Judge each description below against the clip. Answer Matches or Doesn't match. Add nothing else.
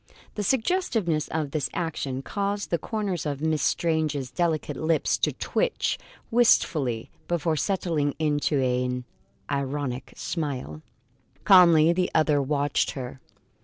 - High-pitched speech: Doesn't match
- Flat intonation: Doesn't match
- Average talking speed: Doesn't match